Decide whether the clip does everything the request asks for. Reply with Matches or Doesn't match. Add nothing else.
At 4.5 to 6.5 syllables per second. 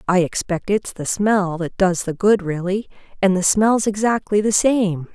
Doesn't match